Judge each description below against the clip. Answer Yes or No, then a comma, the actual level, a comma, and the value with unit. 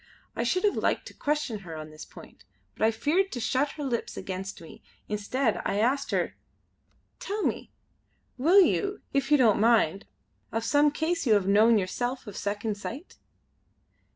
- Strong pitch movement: Yes, wide, 6.3 semitones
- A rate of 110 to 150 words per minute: No, average, 175 wpm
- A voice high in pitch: Yes, high, 235 Hz